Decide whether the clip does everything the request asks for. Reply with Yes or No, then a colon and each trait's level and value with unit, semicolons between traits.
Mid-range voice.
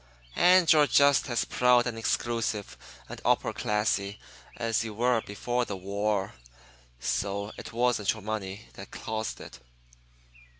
No: low, 110 Hz